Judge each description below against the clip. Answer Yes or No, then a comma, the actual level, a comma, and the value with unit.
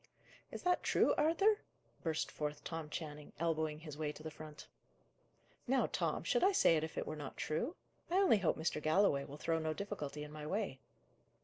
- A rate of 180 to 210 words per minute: Yes, average, 195 wpm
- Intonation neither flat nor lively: Yes, average, 5.0 semitones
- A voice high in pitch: No, medium, 155 Hz